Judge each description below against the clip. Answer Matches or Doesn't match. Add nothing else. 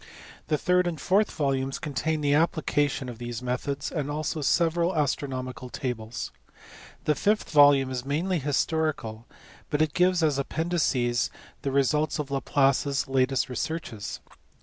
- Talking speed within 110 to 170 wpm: Matches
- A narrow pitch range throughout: Doesn't match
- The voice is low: Doesn't match